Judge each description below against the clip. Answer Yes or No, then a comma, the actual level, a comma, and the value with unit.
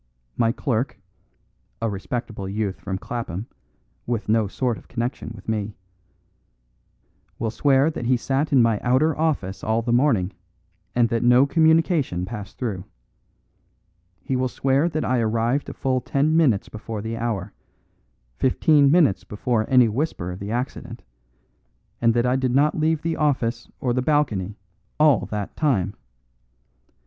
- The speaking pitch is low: Yes, low, 120 Hz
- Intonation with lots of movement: No, average, 4.3 semitones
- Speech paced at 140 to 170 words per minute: Yes, average, 150 wpm